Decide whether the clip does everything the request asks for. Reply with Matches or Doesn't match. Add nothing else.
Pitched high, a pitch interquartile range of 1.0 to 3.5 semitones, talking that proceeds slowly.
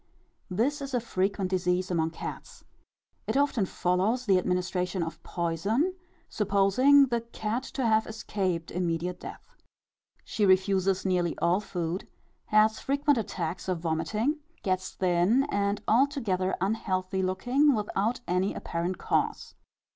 Doesn't match